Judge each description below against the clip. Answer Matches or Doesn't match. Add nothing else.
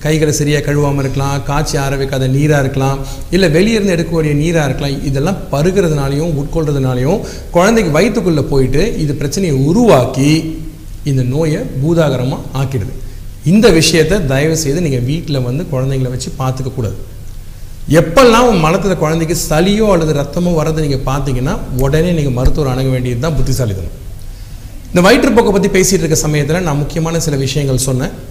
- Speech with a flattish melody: Doesn't match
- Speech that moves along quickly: Matches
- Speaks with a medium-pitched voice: Matches